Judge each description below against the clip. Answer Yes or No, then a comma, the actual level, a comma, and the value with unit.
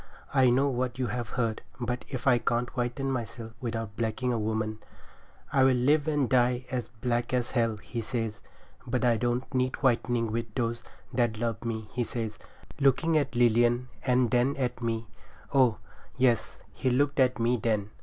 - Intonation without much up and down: Yes, narrow, 1.8 semitones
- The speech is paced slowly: No, average, 170 wpm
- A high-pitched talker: No, low, 120 Hz